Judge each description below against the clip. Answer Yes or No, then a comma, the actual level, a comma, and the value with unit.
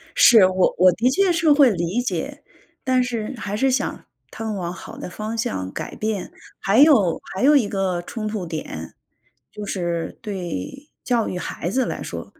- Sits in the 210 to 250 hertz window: Yes, high, 215 Hz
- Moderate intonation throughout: No, wide, 5.7 semitones